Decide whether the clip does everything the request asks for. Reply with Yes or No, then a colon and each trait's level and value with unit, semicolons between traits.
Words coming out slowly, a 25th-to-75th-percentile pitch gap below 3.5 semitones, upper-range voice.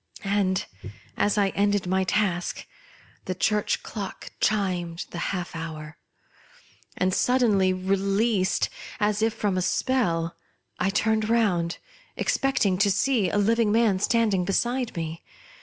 Yes: slow, 125 wpm; average, 3.0 semitones; high, 195 Hz